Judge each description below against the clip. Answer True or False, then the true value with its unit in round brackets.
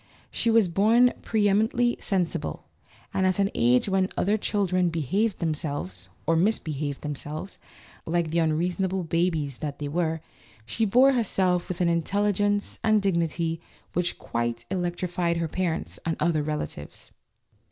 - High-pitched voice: False (175 Hz)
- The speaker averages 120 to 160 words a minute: True (140 wpm)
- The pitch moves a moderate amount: True (3.9 semitones)